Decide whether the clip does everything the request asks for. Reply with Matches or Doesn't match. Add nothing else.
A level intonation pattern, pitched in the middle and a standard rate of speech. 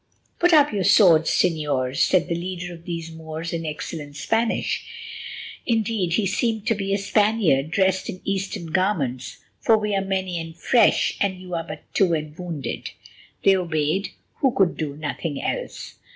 Doesn't match